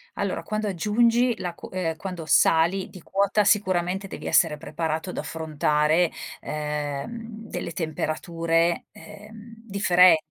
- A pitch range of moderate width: Yes, average, 4.3 semitones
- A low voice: No, medium, 180 Hz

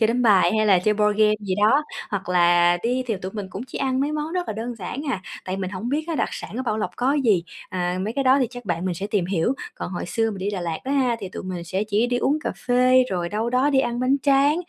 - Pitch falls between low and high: No, high, 215 Hz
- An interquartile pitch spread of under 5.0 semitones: No, wide, 5.5 semitones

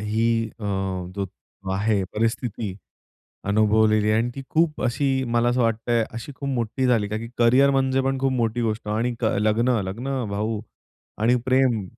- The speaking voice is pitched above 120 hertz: No, low, 115 Hz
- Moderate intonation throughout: Yes, average, 3.1 semitones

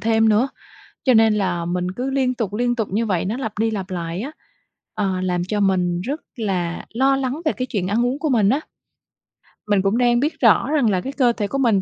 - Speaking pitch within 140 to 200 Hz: No, high, 220 Hz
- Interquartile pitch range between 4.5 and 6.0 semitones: Yes, average, 4.9 semitones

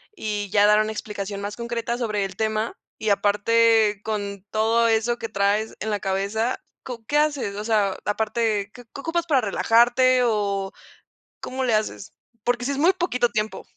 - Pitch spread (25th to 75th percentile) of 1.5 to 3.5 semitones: Yes, narrow, 2.6 semitones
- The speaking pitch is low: No, high, 220 Hz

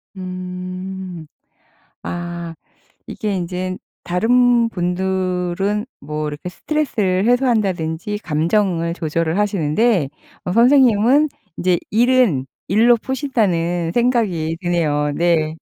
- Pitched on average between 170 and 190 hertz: Yes, medium, 185 Hz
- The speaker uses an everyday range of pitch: Yes, average, 4.7 semitones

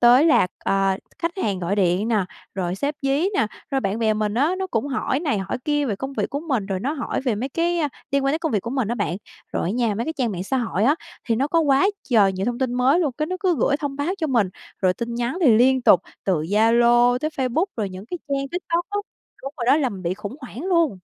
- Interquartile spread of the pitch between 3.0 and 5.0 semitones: No, wide, 5.6 semitones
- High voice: Yes, very high, 250 Hz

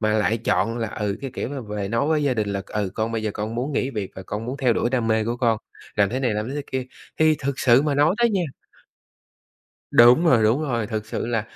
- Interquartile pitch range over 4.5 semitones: No, average, 3.8 semitones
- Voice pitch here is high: No, low, 115 Hz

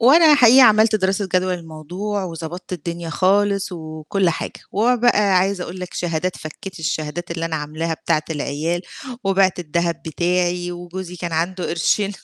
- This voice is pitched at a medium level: Yes, medium, 180 Hz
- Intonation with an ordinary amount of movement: Yes, average, 3.0 semitones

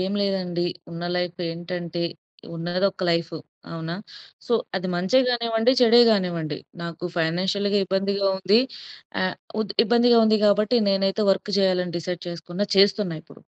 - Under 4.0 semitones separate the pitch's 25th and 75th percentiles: Yes, average, 2.8 semitones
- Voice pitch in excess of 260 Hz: No, high, 190 Hz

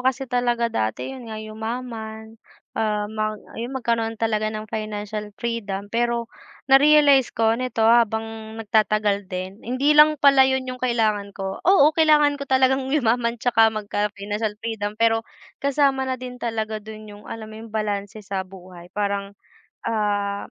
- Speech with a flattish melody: No, average, 3.2 semitones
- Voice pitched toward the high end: Yes, high, 225 Hz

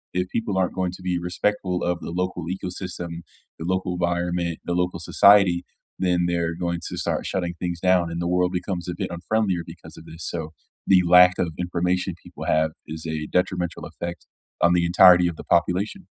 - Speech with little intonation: Yes, narrow, 1.1 semitones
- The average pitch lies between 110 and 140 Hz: No, very low, 90 Hz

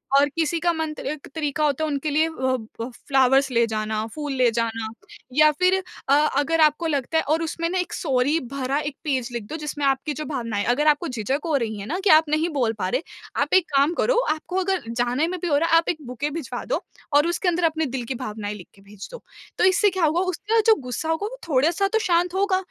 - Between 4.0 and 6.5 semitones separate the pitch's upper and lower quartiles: Yes, average, 4.5 semitones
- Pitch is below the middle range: No, very high, 300 Hz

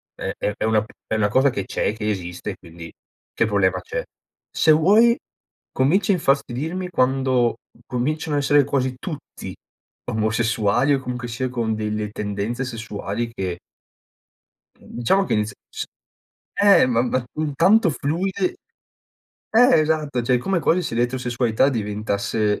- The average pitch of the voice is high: No, low, 125 Hz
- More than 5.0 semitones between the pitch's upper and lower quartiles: Yes, wide, 5.5 semitones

